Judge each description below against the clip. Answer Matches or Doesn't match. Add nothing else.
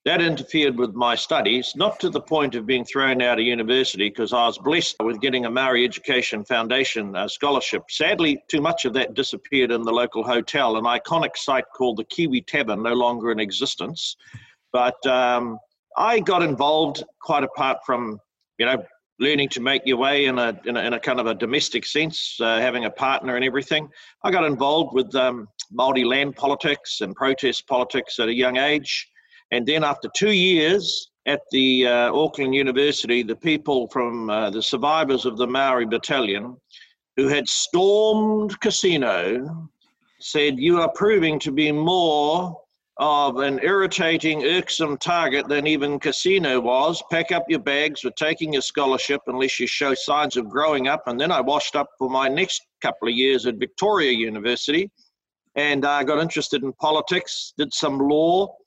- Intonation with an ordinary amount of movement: Matches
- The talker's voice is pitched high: Doesn't match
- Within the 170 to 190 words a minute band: Matches